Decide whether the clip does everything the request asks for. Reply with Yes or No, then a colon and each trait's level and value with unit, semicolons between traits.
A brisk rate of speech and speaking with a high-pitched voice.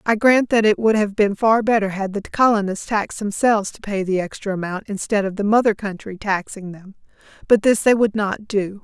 Yes: fast, 215 wpm; high, 205 Hz